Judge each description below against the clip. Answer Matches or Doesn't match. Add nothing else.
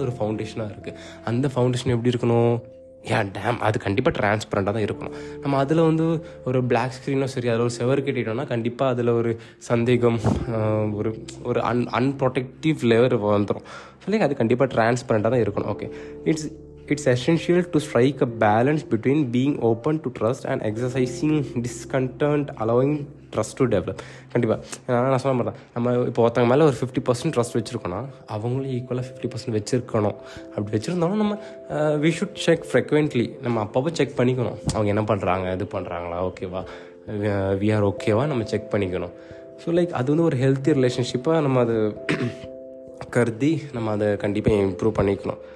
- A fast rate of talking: Matches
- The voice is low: Matches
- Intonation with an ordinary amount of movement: Matches